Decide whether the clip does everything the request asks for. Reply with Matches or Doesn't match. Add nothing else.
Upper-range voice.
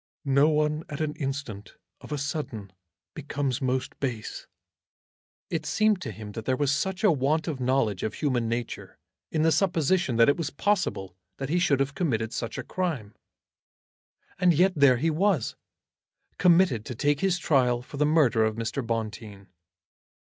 Doesn't match